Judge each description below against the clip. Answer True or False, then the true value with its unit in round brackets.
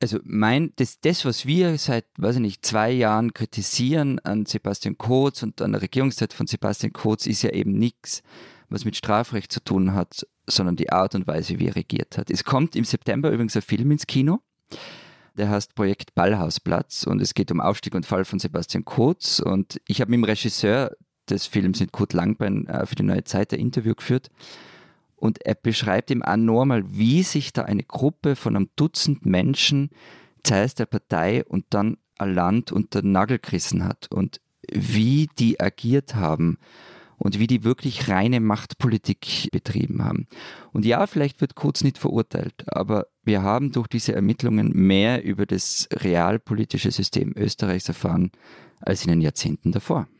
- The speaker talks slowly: False (175 wpm)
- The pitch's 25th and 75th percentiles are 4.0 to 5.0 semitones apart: True (4.4 semitones)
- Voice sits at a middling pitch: False (115 Hz)